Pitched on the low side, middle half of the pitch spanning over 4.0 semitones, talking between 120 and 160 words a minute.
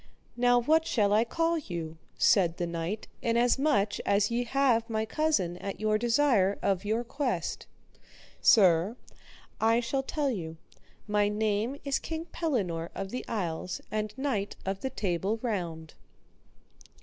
No: high, 215 Hz; average, 4.4 semitones; average, 140 wpm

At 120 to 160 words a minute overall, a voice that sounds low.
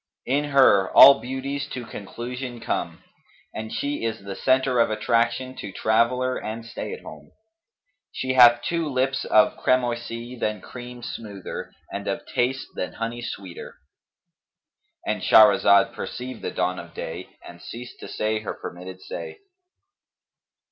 Yes: average, 140 wpm; low, 120 Hz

